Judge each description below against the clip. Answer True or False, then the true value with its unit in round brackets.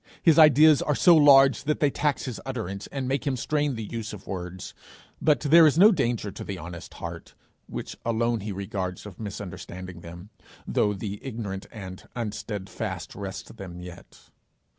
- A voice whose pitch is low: True (110 Hz)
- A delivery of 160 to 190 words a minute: True (170 wpm)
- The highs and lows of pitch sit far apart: True (6.6 semitones)